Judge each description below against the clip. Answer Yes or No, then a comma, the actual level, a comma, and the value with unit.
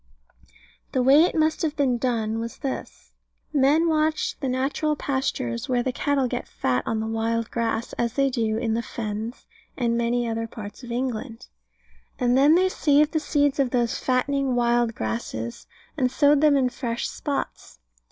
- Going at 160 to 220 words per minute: Yes, average, 170 wpm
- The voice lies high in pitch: Yes, very high, 250 Hz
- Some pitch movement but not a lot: Yes, average, 3.7 semitones